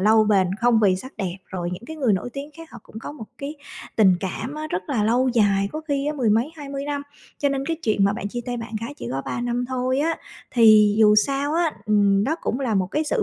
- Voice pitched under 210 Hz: No, high, 240 Hz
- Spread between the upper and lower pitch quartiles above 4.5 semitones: Yes, average, 5.3 semitones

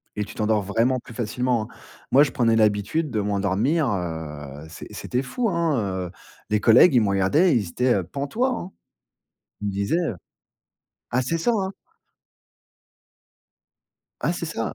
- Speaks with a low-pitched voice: Yes, low, 115 Hz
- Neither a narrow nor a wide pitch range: No, wide, 6.0 semitones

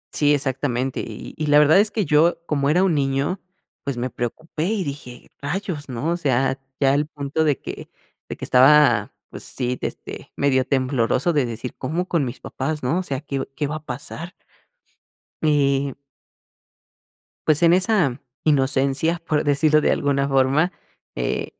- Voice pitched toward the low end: No, medium, 145 Hz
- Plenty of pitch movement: No, average, 2.9 semitones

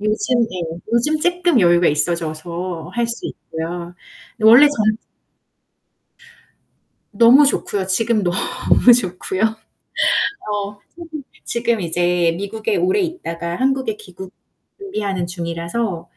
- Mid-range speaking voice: No, high, 205 Hz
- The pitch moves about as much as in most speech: No, wide, 5.8 semitones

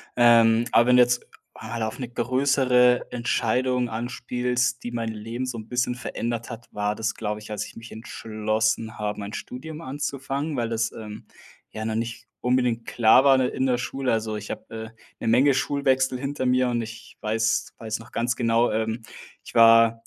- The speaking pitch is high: No, low, 120 Hz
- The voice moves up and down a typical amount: No, narrow, 2.2 semitones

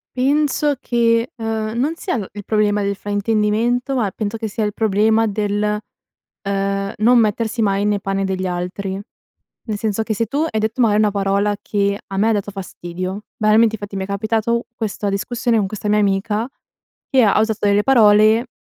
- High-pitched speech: Yes, high, 210 Hz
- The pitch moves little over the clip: Yes, narrow, 2.2 semitones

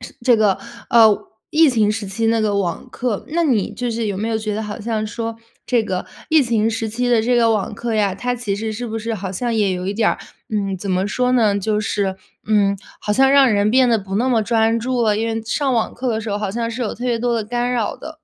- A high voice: Yes, high, 225 Hz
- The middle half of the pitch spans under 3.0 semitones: Yes, narrow, 2.5 semitones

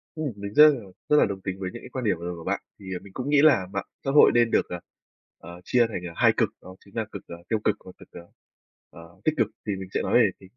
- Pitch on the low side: Yes, low, 100 Hz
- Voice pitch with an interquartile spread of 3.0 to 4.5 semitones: No, average, 5.0 semitones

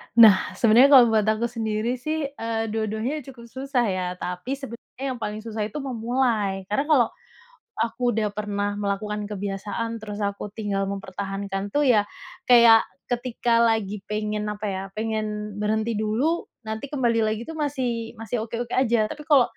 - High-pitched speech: Yes, high, 220 Hz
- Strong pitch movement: No, narrow, 2.5 semitones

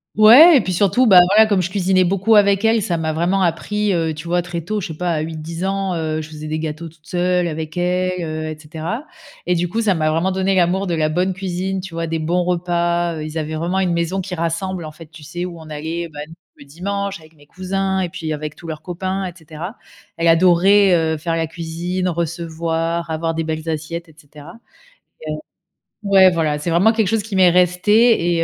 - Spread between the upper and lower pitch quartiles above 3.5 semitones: No, average, 2.8 semitones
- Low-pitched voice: No, medium, 175 Hz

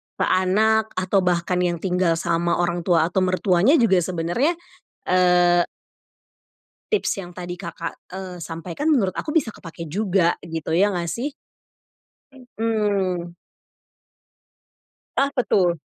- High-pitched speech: No, medium, 180 Hz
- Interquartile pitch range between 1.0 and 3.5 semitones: Yes, average, 2.9 semitones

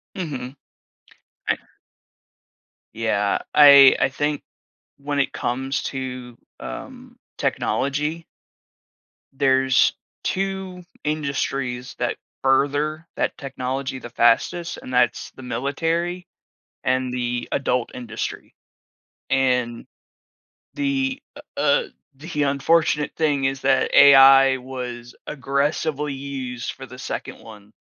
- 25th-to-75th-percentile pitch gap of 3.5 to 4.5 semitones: No, average, 2.9 semitones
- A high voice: No, low, 135 Hz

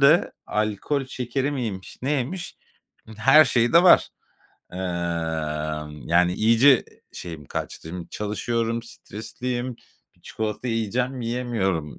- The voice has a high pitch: No, low, 115 Hz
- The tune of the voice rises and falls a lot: Yes, wide, 6.2 semitones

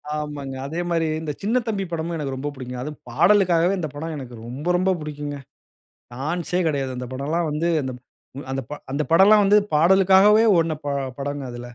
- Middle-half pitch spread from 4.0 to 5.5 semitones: Yes, average, 4.3 semitones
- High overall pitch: No, medium, 155 Hz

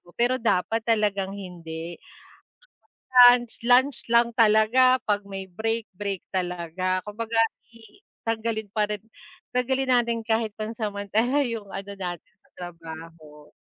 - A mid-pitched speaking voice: No, high, 215 Hz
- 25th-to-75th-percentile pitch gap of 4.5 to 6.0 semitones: No, average, 3.8 semitones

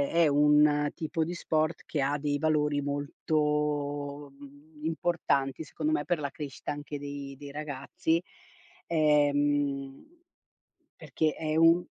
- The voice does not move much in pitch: Yes, narrow, 1.6 semitones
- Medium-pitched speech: Yes, medium, 150 Hz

